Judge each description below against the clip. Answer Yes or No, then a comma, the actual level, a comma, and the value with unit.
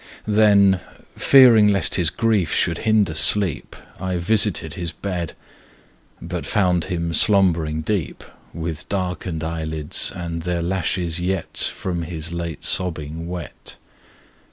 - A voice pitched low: Yes, very low, 90 Hz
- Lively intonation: No, average, 2.9 semitones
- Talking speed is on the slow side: Yes, slow, 120 wpm